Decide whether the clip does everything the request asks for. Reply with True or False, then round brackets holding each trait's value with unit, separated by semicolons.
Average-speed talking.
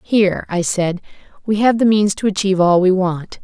False (210 wpm)